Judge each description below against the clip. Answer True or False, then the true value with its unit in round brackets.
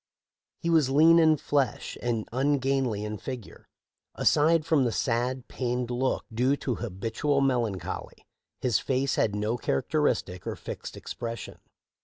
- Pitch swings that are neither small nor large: True (3.3 semitones)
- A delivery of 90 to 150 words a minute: True (135 wpm)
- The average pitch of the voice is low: True (125 Hz)